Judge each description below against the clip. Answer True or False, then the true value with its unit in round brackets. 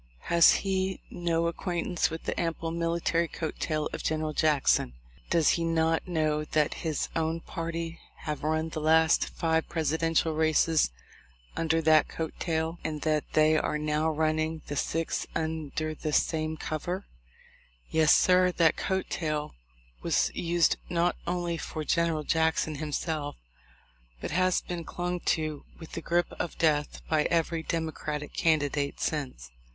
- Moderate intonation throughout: False (1.4 semitones)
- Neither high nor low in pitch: True (160 Hz)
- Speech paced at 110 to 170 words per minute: True (150 wpm)